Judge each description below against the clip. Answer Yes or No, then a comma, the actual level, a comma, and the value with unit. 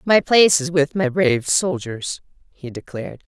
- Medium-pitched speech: Yes, medium, 180 Hz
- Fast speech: No, average, 160 wpm